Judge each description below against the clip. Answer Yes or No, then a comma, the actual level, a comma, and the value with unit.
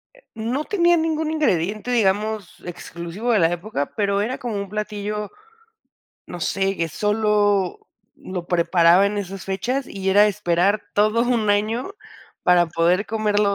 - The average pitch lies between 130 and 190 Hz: No, high, 205 Hz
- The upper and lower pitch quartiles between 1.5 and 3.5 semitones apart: Yes, average, 3.1 semitones